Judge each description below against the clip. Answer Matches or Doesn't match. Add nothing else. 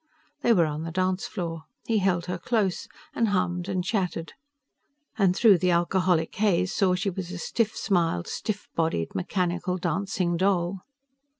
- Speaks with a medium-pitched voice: Matches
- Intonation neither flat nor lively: Doesn't match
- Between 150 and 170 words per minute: Matches